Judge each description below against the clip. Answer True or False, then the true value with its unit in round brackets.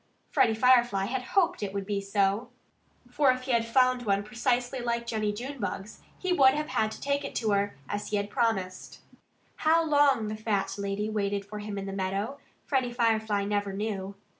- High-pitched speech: True (220 Hz)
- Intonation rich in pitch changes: False (4.0 semitones)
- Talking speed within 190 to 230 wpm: True (195 wpm)